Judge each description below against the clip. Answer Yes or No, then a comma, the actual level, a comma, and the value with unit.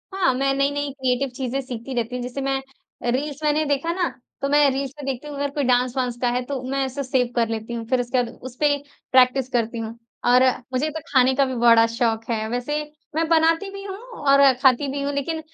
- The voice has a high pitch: Yes, very high, 270 Hz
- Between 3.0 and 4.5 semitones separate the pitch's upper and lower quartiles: No, narrow, 2.6 semitones